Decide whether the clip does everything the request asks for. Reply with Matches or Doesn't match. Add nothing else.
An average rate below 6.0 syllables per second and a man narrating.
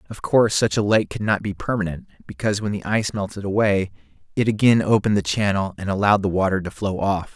Doesn't match